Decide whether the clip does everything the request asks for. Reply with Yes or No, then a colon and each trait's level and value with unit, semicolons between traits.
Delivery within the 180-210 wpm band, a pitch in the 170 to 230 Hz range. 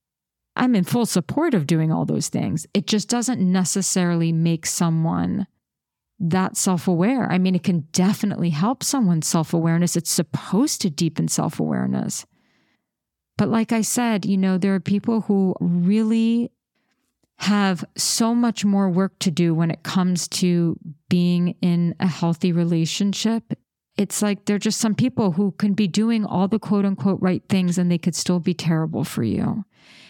No: average, 170 wpm; high, 190 Hz